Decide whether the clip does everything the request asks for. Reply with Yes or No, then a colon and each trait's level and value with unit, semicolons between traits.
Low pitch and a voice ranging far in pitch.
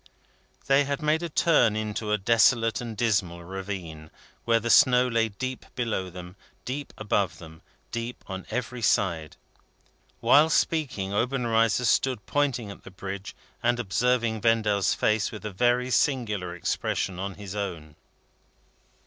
No: low, 110 Hz; average, 4.4 semitones